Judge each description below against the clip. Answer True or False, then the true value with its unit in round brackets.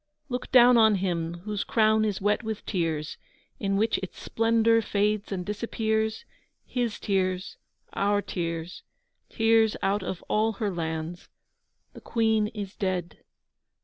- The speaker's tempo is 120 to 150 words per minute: True (135 wpm)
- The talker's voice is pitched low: False (205 Hz)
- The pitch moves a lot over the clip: False (3.1 semitones)